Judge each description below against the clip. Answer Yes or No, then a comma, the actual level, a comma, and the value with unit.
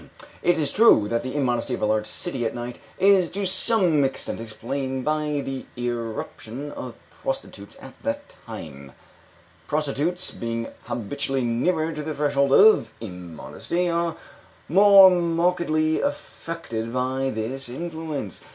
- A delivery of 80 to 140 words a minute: Yes, slow, 135 wpm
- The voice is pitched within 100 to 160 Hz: Yes, medium, 140 Hz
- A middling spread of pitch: No, wide, 6.2 semitones